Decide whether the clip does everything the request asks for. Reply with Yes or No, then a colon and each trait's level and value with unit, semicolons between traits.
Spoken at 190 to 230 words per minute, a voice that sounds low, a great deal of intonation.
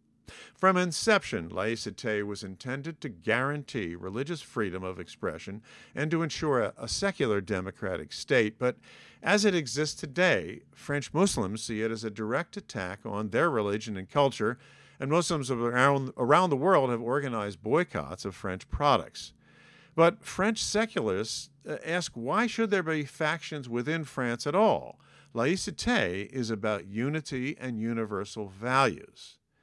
No: average, 140 wpm; low, 130 Hz; wide, 7.0 semitones